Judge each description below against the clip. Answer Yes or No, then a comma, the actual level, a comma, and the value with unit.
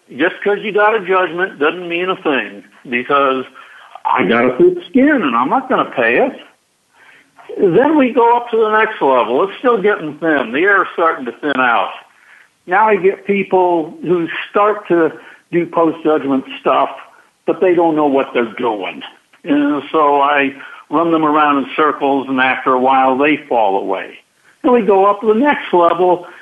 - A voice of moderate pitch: Yes, medium, 175 Hz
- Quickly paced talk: No, average, 190 wpm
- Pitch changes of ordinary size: No, wide, 6.7 semitones